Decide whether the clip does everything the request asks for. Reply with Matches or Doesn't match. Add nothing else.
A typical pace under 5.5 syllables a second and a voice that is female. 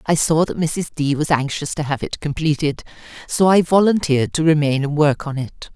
Matches